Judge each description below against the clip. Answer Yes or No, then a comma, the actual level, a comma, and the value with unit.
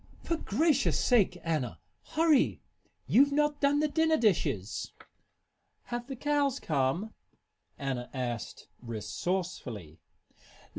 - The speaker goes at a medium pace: No, slow, 100 wpm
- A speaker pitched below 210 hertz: No, high, 215 Hz